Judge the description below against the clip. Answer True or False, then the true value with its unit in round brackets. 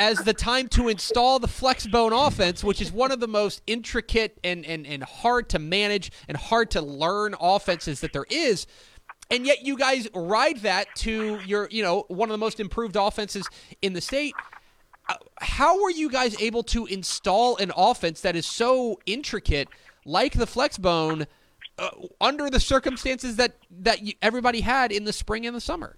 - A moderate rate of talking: True (180 wpm)